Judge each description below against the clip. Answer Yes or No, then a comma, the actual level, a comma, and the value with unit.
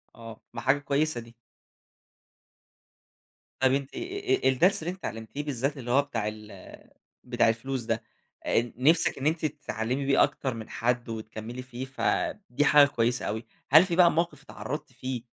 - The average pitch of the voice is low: Yes, low, 130 Hz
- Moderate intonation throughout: Yes, average, 4.1 semitones